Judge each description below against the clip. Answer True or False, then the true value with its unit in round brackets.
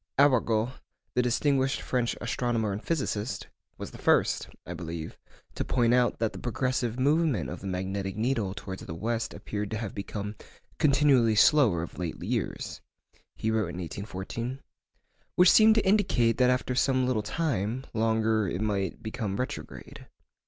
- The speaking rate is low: False (155 wpm)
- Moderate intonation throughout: True (4.2 semitones)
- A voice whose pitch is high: False (115 Hz)